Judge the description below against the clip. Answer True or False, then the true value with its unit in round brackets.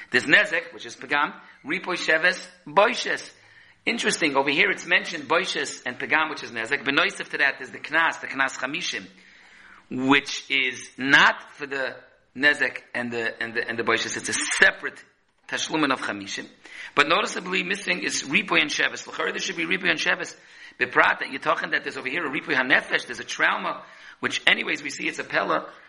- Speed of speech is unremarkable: True (190 wpm)